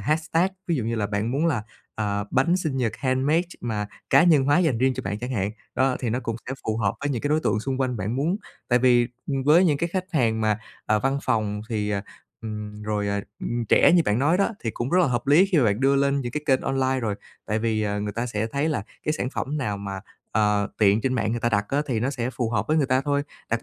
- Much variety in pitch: No, average, 4.8 semitones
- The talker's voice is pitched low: Yes, low, 125 Hz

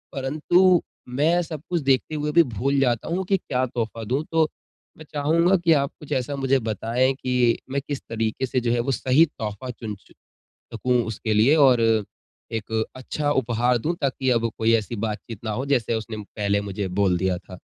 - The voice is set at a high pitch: No, low, 125 Hz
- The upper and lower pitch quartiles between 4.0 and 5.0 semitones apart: Yes, average, 4.5 semitones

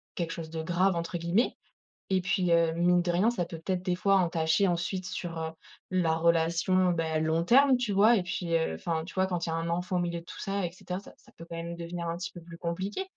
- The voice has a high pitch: No, medium, 175 Hz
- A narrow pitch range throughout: Yes, narrow, 1.9 semitones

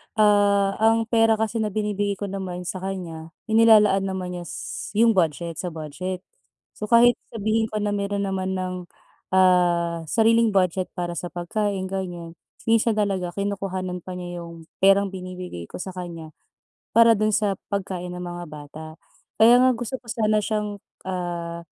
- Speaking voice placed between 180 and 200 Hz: Yes, high, 190 Hz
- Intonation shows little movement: No, average, 3.1 semitones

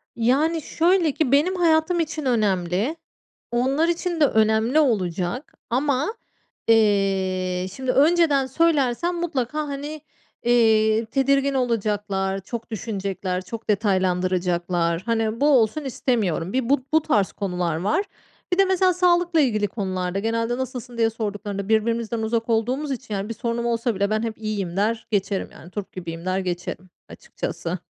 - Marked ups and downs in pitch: Yes, wide, 5.9 semitones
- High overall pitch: Yes, high, 230 Hz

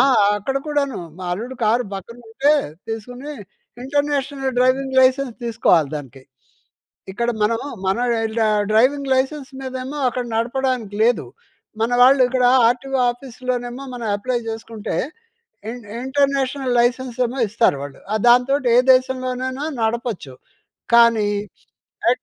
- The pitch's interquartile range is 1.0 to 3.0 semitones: Yes, narrow, 2.5 semitones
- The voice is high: Yes, very high, 250 Hz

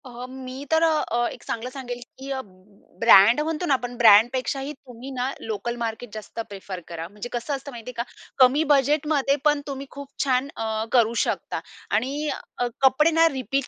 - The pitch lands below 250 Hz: No, very high, 255 Hz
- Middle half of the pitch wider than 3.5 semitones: No, average, 3.0 semitones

